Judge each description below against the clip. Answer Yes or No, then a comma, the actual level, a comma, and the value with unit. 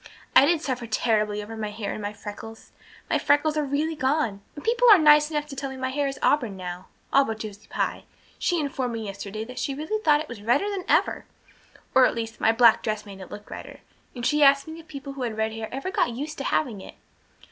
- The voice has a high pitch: Yes, very high, 260 Hz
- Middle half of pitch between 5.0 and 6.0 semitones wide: Yes, average, 5.3 semitones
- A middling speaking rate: No, fast, 245 wpm